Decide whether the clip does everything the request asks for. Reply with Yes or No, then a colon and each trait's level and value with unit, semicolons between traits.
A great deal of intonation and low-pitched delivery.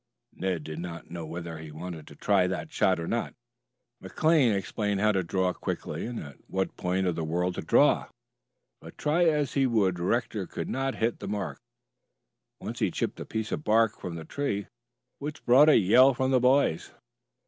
Yes: wide, 6.4 semitones; low, 100 Hz